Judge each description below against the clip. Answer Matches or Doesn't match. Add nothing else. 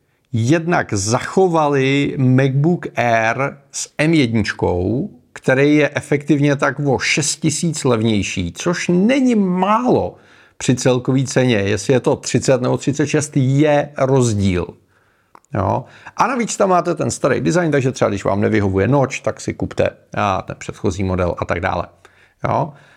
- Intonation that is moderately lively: Matches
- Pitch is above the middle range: Doesn't match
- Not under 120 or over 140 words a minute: Matches